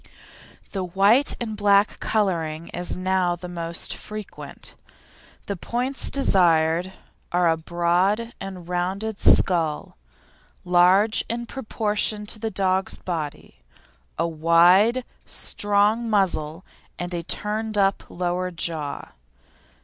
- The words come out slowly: Yes, slow, 110 wpm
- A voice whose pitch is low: No, medium, 185 Hz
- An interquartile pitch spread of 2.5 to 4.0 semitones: Yes, average, 3.5 semitones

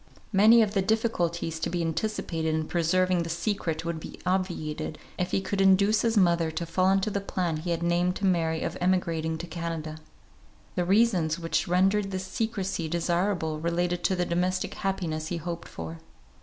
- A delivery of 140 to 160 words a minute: No, average, 180 wpm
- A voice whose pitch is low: No, medium, 175 Hz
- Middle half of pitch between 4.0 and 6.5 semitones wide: No, average, 2.7 semitones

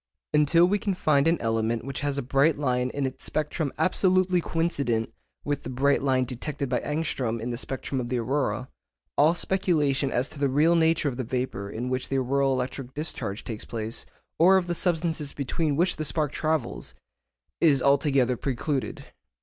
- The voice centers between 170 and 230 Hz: No, medium, 140 Hz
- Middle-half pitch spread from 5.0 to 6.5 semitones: No, average, 3.9 semitones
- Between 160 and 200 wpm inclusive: Yes, average, 180 wpm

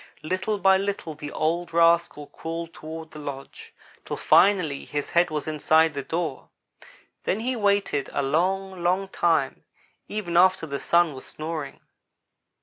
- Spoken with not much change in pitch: No, average, 3.5 semitones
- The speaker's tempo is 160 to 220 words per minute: No, average, 145 wpm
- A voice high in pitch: No, medium, 165 Hz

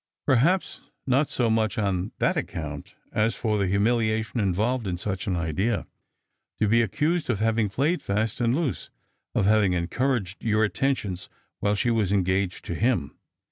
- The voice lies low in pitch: Yes, low, 110 Hz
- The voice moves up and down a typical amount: Yes, average, 3.9 semitones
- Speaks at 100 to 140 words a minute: No, average, 165 wpm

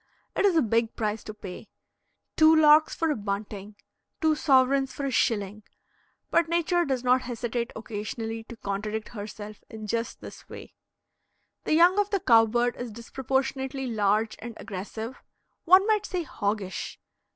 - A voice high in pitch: Yes, high, 235 Hz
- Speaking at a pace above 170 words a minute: No, average, 155 wpm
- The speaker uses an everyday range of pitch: No, wide, 5.8 semitones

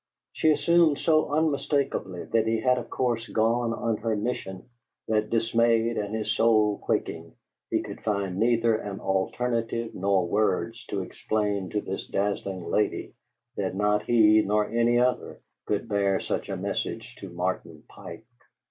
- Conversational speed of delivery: Yes, average, 150 wpm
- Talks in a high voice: No, low, 110 Hz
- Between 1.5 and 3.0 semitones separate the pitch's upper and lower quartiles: Yes, narrow, 2.4 semitones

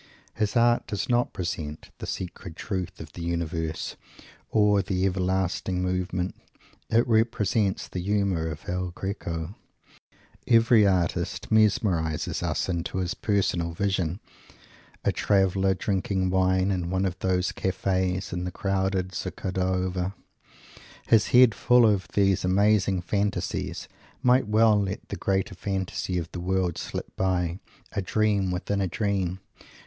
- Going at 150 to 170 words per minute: No, slow, 135 wpm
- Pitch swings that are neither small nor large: No, narrow, 2.0 semitones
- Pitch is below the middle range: Yes, very low, 95 Hz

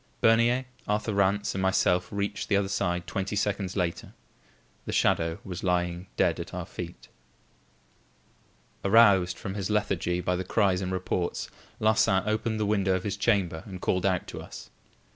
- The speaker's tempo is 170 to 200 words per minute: No, average, 160 wpm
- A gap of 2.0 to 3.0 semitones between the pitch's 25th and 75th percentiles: Yes, narrow, 2.4 semitones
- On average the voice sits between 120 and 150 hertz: No, very low, 95 Hz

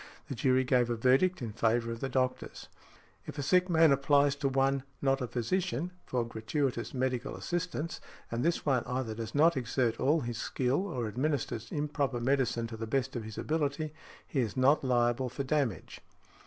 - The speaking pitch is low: Yes, low, 130 Hz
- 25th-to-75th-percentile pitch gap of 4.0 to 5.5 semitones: No, average, 3.4 semitones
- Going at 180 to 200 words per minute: Yes, average, 185 wpm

